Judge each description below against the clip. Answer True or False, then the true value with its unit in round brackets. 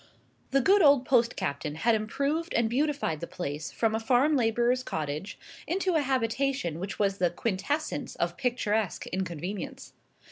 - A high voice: True (230 Hz)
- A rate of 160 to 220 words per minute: False (150 wpm)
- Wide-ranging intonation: True (6.7 semitones)